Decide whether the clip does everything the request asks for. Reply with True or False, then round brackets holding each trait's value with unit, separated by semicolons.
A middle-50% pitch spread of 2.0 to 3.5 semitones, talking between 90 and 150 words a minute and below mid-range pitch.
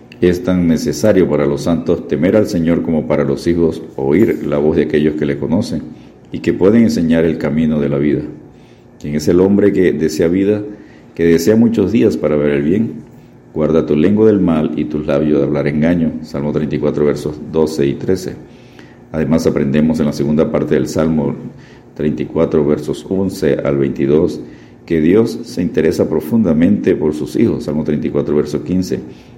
False (2.9 semitones; 180 wpm; 75 Hz)